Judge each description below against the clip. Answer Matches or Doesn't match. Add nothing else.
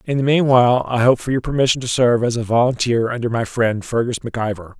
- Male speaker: Matches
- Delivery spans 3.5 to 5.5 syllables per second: Doesn't match